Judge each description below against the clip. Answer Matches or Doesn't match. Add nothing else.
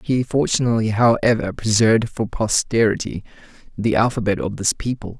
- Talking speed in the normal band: Doesn't match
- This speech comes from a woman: Doesn't match